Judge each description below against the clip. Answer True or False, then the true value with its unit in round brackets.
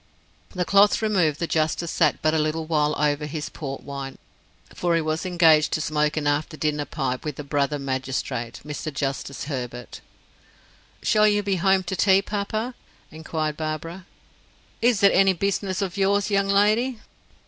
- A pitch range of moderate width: True (4.7 semitones)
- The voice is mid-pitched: True (160 Hz)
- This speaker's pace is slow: False (165 wpm)